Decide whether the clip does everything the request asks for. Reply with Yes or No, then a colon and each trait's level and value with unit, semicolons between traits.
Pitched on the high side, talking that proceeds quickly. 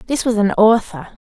No: high, 215 Hz; average, 195 wpm